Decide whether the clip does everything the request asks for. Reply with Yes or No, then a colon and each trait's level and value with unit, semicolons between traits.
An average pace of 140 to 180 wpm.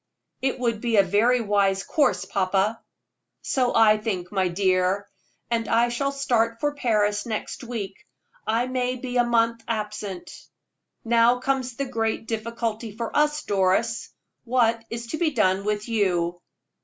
Yes: average, 150 wpm